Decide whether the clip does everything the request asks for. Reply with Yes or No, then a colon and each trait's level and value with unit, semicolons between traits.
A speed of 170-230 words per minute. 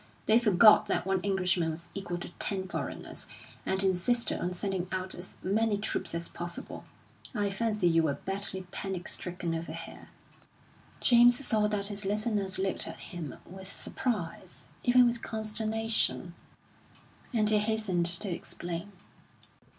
No: average, 145 wpm